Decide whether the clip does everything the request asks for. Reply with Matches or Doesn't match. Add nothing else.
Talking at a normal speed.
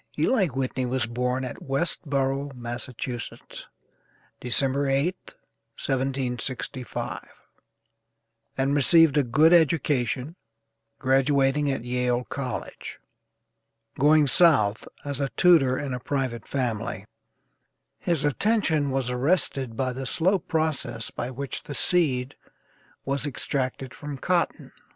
Doesn't match